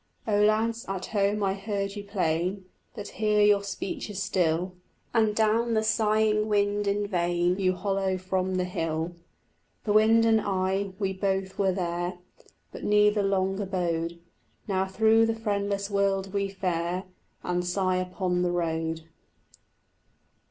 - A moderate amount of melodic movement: No, narrow, 2.2 semitones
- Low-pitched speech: No, high, 195 Hz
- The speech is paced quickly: No, average, 145 wpm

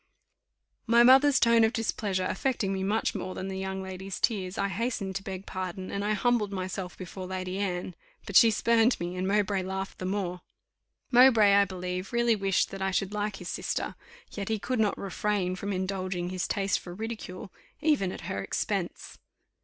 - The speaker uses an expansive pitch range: No, narrow, 2.6 semitones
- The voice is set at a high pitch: Yes, high, 195 Hz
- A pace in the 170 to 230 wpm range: Yes, average, 185 wpm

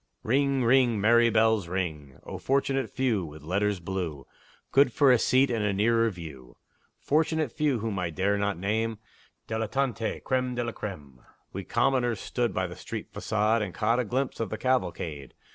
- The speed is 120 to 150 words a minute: No, average, 175 wpm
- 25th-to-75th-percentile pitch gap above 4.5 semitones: Yes, average, 5.1 semitones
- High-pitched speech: No, low, 110 Hz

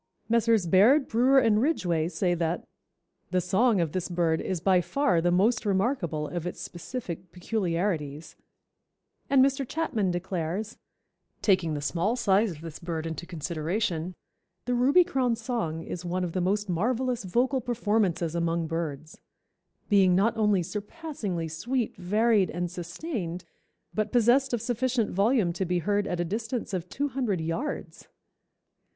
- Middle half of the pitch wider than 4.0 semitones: Yes, wide, 5.4 semitones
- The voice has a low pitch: No, high, 190 Hz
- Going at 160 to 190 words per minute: No, average, 150 wpm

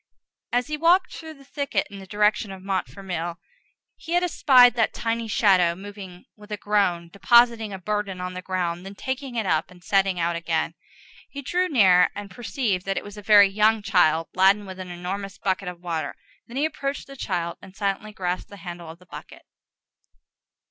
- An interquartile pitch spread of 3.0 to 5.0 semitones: Yes, average, 3.9 semitones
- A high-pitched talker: Yes, high, 200 Hz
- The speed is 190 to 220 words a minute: Yes, average, 195 wpm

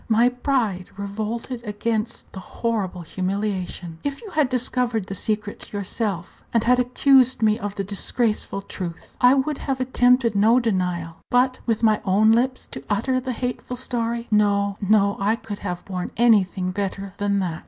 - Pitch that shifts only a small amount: No, average, 3.8 semitones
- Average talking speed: Yes, average, 165 wpm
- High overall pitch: Yes, high, 215 Hz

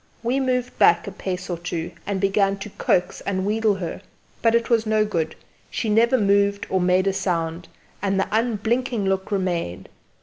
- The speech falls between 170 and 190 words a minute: Yes, average, 180 wpm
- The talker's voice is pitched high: Yes, high, 200 Hz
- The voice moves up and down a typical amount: Yes, average, 3.1 semitones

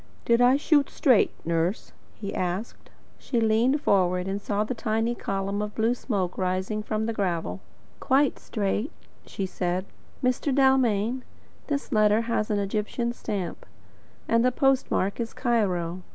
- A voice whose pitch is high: Yes, high, 215 Hz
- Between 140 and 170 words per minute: Yes, average, 145 wpm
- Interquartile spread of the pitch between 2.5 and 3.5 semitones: No, average, 4.0 semitones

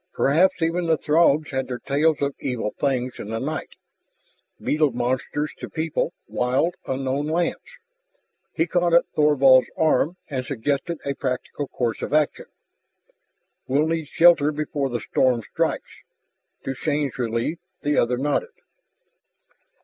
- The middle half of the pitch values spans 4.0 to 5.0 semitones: No, average, 3.6 semitones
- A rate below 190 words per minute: Yes, slow, 135 wpm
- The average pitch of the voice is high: No, medium, 145 Hz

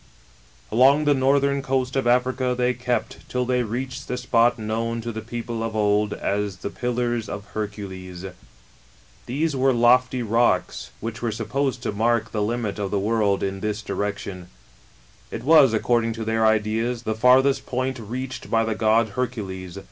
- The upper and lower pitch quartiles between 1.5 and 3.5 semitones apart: Yes, average, 3.0 semitones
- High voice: No, low, 115 Hz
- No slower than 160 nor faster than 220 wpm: Yes, average, 170 wpm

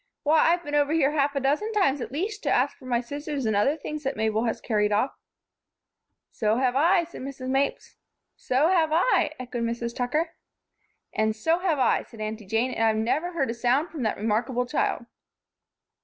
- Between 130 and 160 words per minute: No, average, 200 wpm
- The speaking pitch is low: No, very high, 265 Hz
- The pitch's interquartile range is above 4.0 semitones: Yes, average, 4.8 semitones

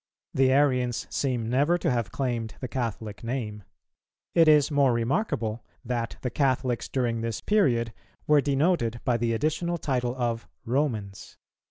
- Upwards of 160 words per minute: No, average, 145 wpm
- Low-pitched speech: Yes, low, 125 Hz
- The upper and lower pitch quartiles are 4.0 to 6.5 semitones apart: No, average, 3.5 semitones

